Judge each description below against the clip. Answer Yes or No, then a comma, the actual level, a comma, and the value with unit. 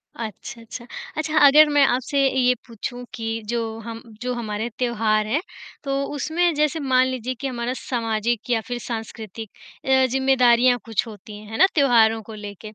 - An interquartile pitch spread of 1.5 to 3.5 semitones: Yes, average, 2.9 semitones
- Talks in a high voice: Yes, high, 240 Hz